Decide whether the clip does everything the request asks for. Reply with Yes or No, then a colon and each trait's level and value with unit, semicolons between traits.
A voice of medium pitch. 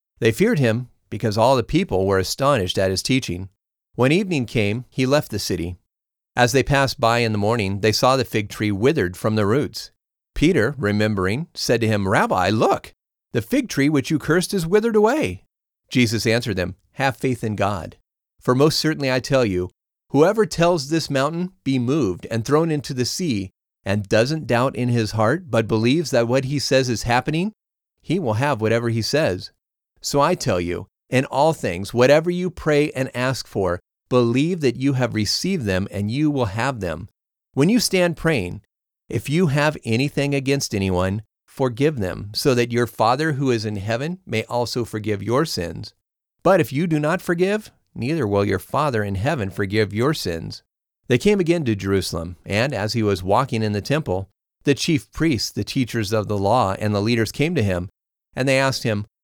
No: low, 120 Hz